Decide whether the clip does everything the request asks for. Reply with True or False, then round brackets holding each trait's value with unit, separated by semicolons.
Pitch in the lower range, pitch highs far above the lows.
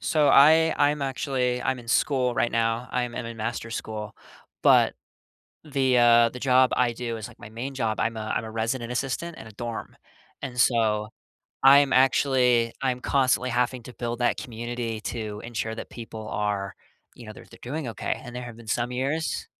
False (120 Hz; 2.4 semitones)